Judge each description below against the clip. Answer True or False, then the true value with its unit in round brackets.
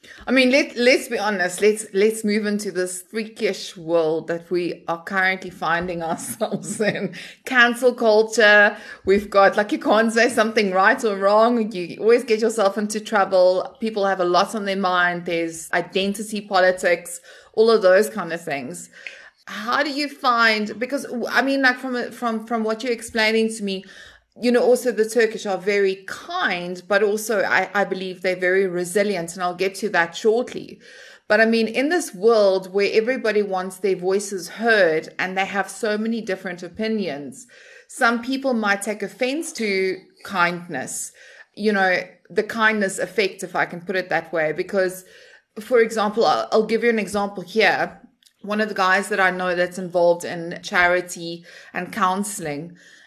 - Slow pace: False (175 wpm)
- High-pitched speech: True (205 Hz)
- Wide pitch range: False (3.5 semitones)